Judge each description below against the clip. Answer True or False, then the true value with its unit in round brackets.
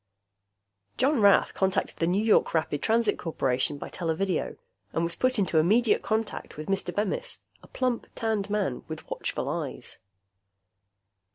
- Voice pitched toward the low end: False (195 Hz)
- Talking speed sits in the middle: True (145 wpm)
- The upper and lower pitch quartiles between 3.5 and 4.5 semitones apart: False (5.1 semitones)